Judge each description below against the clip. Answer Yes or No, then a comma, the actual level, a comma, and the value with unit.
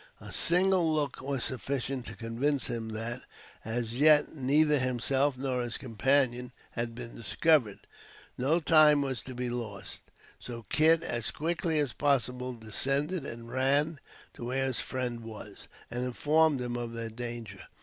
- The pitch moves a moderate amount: Yes, average, 3.6 semitones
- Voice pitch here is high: No, low, 130 Hz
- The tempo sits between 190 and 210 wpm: No, average, 150 wpm